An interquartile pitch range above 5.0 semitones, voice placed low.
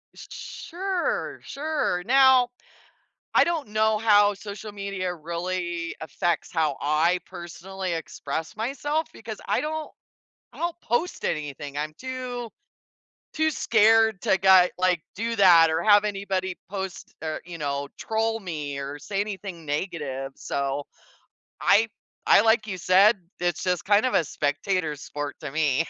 No: wide, 5.6 semitones; high, 190 Hz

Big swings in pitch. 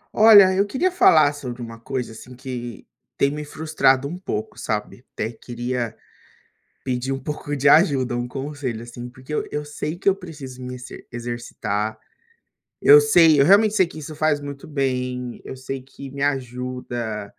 No: average, 3.5 semitones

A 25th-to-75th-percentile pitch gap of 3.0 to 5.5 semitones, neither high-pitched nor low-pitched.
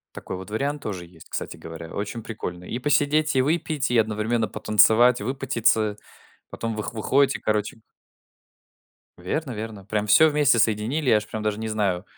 No: average, 4.0 semitones; low, 110 Hz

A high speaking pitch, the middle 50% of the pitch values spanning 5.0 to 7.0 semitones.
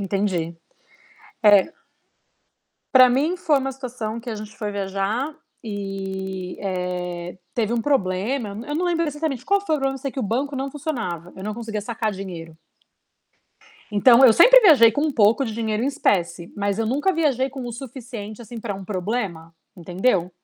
Yes: high, 225 Hz; wide, 5.6 semitones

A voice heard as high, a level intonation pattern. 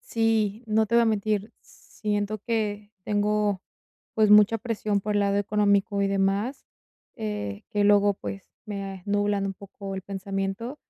Yes: high, 205 Hz; narrow, 1.4 semitones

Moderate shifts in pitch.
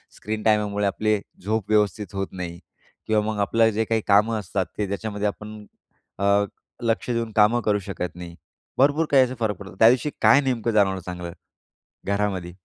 No: narrow, 2.2 semitones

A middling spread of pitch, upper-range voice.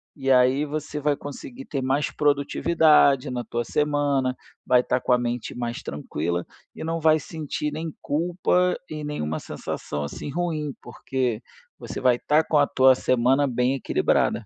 No: average, 3.2 semitones; medium, 140 Hz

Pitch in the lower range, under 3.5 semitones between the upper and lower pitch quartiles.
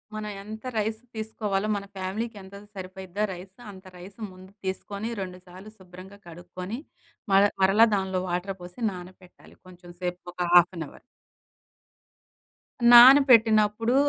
No: high, 190 Hz; average, 2.7 semitones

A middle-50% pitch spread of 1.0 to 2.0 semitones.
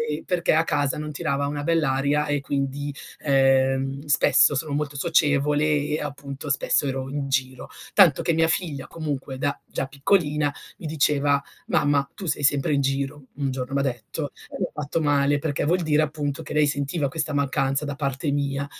Yes: narrow, 1.5 semitones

